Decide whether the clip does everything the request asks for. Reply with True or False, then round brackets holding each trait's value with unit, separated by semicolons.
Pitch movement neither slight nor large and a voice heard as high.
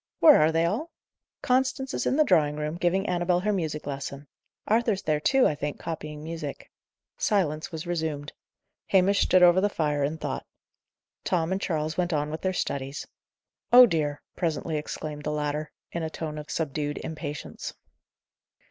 False (3.7 semitones; 160 Hz)